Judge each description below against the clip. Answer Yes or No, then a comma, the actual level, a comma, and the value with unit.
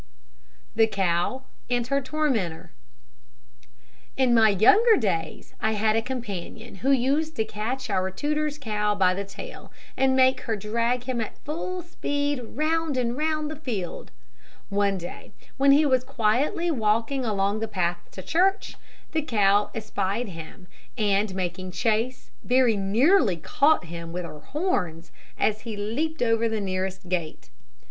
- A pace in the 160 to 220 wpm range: No, average, 150 wpm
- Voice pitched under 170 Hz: No, high, 225 Hz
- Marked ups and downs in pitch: Yes, wide, 5.9 semitones